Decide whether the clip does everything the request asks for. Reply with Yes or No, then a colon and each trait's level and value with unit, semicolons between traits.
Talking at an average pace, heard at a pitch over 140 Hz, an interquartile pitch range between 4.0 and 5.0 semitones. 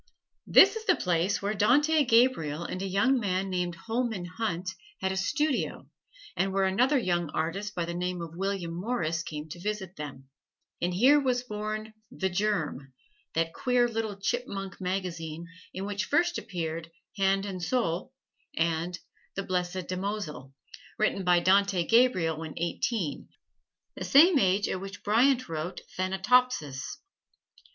Yes: average, 145 wpm; high, 190 Hz; average, 4.4 semitones